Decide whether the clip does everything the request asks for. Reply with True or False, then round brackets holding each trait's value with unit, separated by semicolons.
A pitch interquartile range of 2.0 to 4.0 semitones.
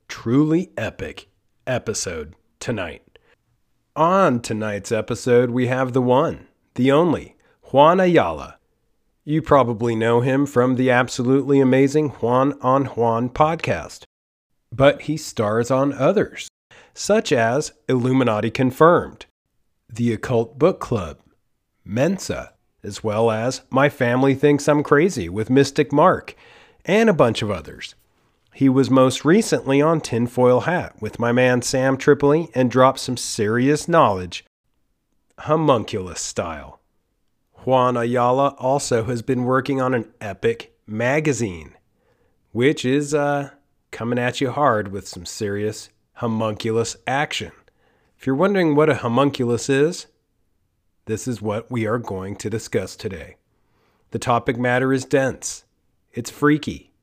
True (3.7 semitones)